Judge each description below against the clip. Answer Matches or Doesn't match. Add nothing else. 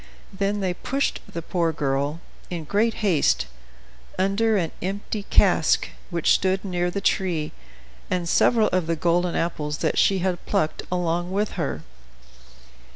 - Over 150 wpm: Doesn't match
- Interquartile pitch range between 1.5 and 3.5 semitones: Matches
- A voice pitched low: Doesn't match